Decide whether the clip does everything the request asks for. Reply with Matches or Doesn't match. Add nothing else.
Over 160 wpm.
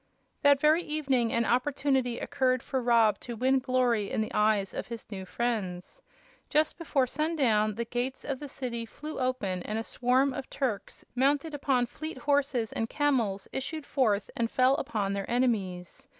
Matches